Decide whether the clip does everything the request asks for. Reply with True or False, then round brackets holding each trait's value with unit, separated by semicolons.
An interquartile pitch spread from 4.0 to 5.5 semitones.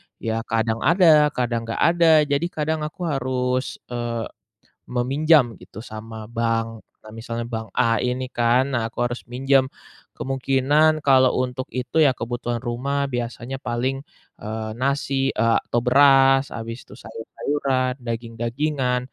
False (2.9 semitones)